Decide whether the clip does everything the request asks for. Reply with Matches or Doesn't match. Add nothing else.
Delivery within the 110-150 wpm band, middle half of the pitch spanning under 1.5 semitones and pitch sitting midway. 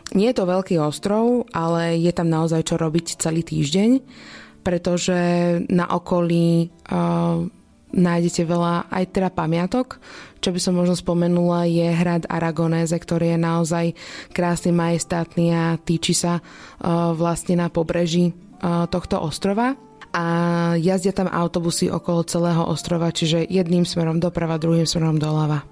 Matches